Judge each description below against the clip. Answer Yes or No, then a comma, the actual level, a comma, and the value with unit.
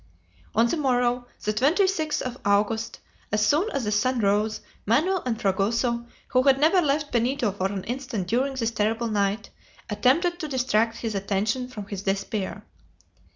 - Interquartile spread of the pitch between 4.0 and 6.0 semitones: Yes, average, 4.3 semitones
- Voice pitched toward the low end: No, high, 235 Hz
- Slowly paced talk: No, average, 160 wpm